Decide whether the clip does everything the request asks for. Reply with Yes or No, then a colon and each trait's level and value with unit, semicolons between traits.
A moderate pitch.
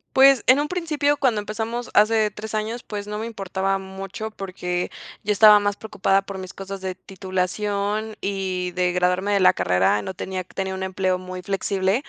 No: high, 195 Hz